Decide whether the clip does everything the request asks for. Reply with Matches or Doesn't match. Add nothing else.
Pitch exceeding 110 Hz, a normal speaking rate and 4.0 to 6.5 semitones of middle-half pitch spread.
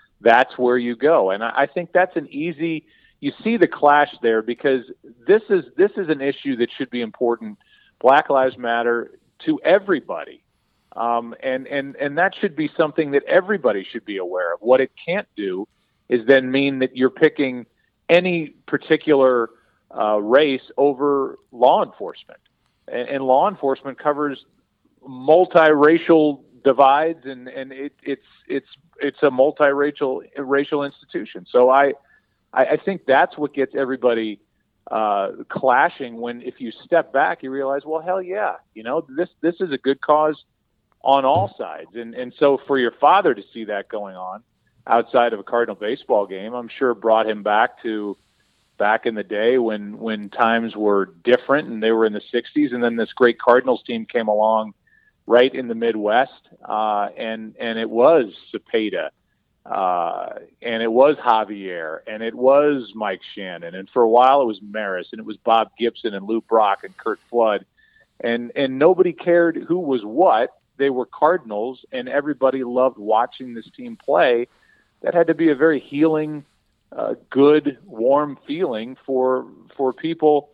Matches